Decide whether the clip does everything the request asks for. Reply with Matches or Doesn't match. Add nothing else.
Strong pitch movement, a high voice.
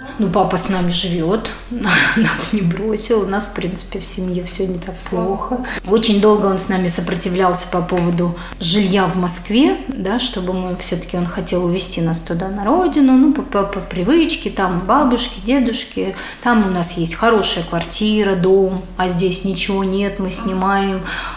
Doesn't match